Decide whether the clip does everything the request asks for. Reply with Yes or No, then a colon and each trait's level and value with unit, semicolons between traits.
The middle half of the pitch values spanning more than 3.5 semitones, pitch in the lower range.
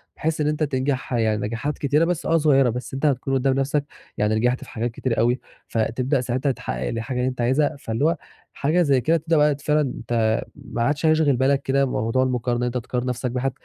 No: average, 3.2 semitones; low, 130 Hz